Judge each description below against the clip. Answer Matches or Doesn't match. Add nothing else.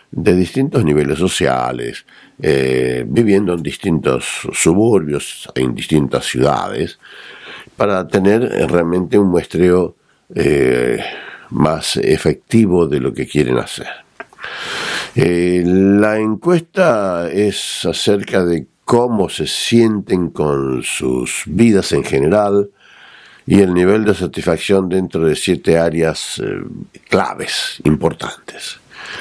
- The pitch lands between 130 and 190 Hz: Doesn't match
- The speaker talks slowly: Matches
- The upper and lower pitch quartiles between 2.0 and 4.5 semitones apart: Doesn't match